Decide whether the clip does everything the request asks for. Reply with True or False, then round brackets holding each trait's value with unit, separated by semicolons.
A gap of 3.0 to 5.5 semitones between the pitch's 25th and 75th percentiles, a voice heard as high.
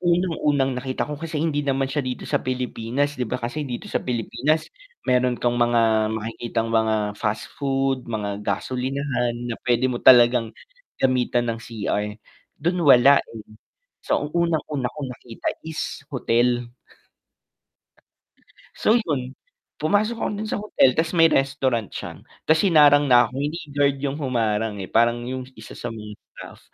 False (3.6 semitones; 130 Hz)